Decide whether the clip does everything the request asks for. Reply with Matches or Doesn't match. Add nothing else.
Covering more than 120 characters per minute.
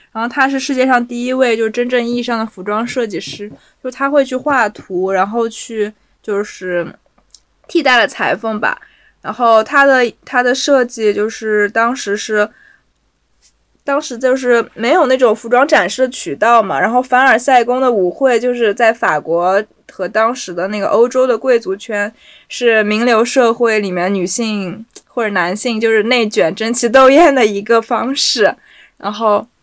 Matches